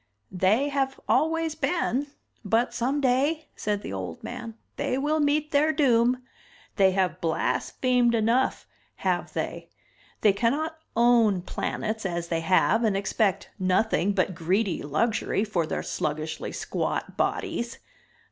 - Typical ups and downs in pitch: No, wide, 6.1 semitones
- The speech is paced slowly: Yes, slow, 130 wpm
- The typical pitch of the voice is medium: No, high, 225 Hz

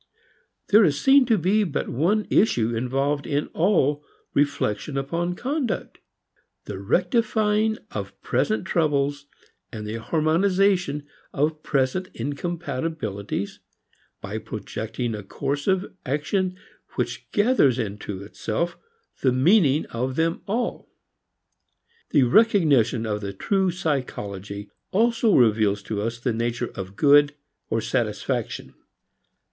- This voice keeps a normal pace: No, slow, 110 wpm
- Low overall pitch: No, medium, 145 Hz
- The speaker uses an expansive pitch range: Yes, wide, 8.0 semitones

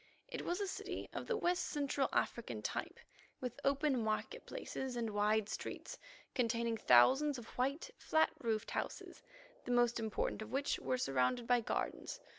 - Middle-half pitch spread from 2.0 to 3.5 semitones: No, average, 4.2 semitones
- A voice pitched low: No, high, 245 Hz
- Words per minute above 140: Yes, average, 160 wpm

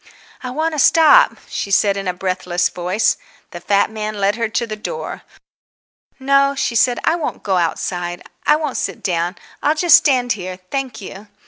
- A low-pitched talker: No, high, 215 Hz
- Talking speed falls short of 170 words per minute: No, average, 185 wpm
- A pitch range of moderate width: No, wide, 6.8 semitones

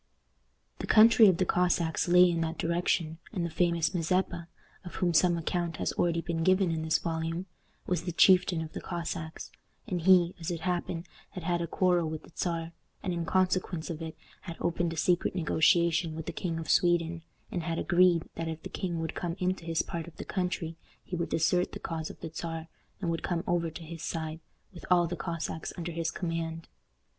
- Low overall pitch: No, medium, 170 Hz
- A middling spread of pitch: No, narrow, 1.5 semitones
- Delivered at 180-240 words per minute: Yes, fast, 205 wpm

